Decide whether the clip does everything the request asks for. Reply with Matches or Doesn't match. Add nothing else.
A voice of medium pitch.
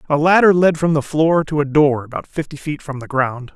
Matches